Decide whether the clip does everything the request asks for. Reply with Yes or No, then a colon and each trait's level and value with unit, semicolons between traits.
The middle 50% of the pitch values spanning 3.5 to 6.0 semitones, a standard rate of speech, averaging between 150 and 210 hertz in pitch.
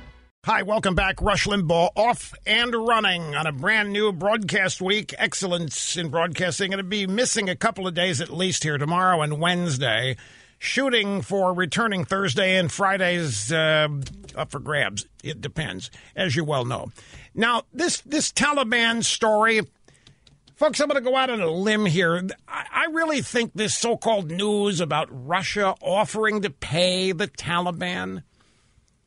Yes: average, 4.5 semitones; average, 155 wpm; high, 190 Hz